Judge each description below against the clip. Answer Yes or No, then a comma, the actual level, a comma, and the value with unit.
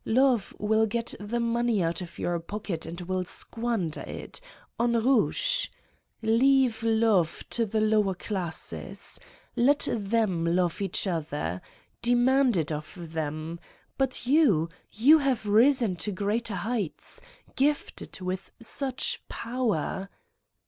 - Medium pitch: No, high, 215 Hz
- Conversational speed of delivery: No, slow, 120 wpm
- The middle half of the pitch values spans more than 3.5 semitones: Yes, average, 5.1 semitones